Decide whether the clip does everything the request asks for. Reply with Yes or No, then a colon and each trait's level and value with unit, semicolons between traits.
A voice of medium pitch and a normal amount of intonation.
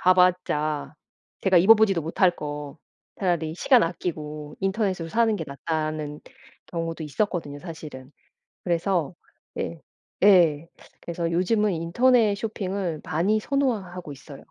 Yes: medium, 170 Hz; average, 4.1 semitones